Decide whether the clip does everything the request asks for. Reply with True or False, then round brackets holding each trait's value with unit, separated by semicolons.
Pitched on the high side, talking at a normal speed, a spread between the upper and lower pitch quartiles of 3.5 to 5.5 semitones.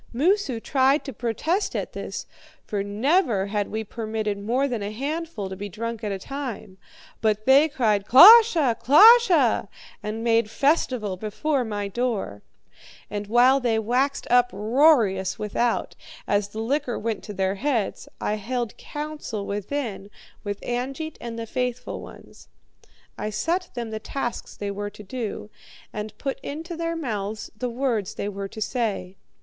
True (230 Hz; 155 wpm; 4.7 semitones)